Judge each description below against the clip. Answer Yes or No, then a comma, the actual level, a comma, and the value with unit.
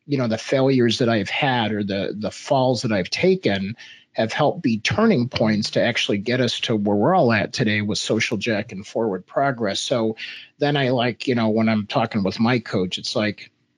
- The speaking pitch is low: Yes, low, 115 Hz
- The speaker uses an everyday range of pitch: Yes, average, 3.2 semitones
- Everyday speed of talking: No, fast, 215 wpm